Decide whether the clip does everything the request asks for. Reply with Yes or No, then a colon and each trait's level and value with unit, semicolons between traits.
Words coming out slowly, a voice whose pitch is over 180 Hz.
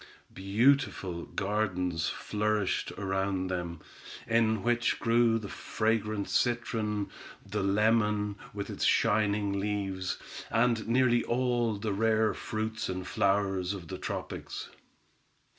No: slow, 110 wpm; low, 105 Hz